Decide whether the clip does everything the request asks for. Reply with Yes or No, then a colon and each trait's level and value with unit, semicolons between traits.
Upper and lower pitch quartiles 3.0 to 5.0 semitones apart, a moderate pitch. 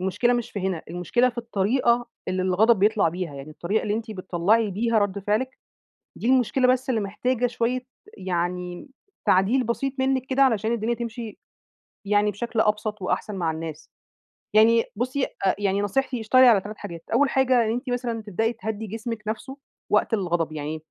No: average, 4.1 semitones; high, 220 Hz